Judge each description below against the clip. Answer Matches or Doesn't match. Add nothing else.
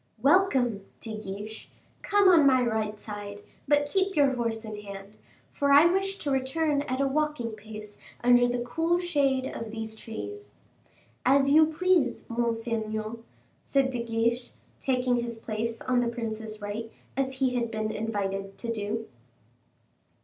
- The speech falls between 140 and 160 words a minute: Matches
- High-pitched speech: Matches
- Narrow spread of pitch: Doesn't match